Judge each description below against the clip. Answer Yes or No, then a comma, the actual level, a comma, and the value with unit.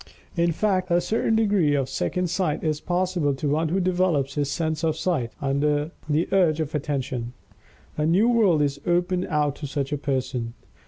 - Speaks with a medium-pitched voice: Yes, medium, 155 Hz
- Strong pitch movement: No, average, 3.9 semitones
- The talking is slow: No, average, 180 wpm